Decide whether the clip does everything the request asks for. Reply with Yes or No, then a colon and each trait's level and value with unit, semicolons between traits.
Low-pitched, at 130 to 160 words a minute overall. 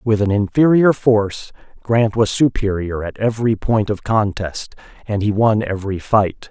Yes: low, 105 Hz; average, 155 wpm